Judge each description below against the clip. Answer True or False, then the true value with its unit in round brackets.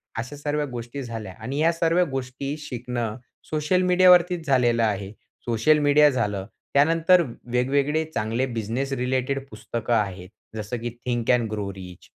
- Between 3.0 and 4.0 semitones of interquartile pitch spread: False (4.6 semitones)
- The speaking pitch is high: False (125 Hz)